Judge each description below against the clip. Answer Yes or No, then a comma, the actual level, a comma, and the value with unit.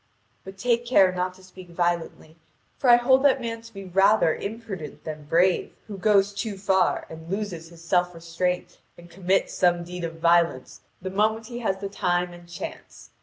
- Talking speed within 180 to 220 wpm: Yes, average, 185 wpm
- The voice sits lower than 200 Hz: Yes, medium, 185 Hz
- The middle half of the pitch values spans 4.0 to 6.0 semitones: No, average, 3.2 semitones